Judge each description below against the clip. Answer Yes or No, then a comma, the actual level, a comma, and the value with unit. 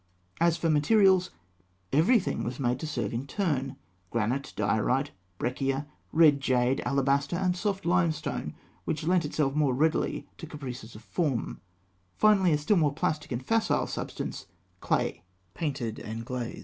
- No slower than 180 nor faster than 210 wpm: No, average, 145 wpm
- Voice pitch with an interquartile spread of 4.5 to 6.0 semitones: Yes, average, 5.1 semitones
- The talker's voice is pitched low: No, medium, 145 Hz